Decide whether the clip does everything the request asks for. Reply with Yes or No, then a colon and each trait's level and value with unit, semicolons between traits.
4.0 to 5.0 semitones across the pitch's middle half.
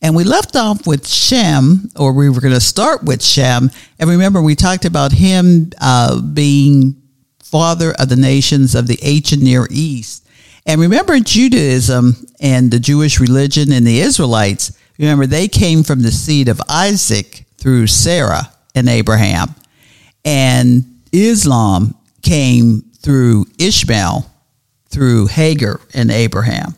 Yes: average, 4.5 semitones